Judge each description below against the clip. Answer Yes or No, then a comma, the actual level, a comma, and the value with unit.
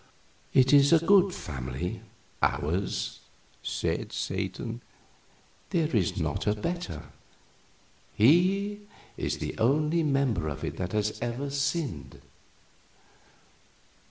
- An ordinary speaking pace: No, slow, 100 wpm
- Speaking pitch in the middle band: No, low, 130 Hz